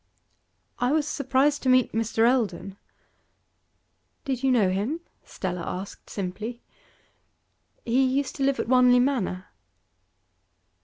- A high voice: Yes, very high, 250 Hz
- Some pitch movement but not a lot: Yes, average, 4.5 semitones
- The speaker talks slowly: Yes, slow, 115 wpm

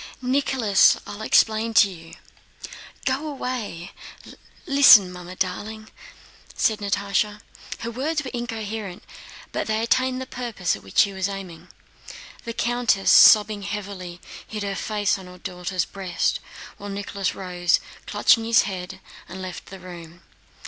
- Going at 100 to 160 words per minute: Yes, slow, 135 wpm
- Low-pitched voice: No, high, 205 Hz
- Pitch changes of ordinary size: Yes, average, 3.8 semitones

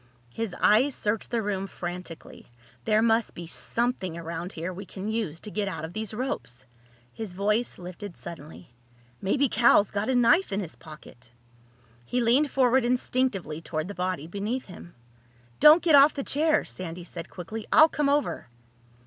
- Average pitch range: No, wide, 5.8 semitones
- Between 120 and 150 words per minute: No, average, 165 wpm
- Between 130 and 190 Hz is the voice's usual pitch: No, high, 205 Hz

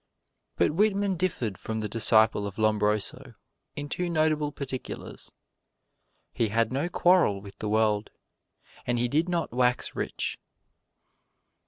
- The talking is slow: Yes, slow, 130 wpm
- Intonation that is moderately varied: No, wide, 6.7 semitones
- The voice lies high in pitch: No, low, 120 Hz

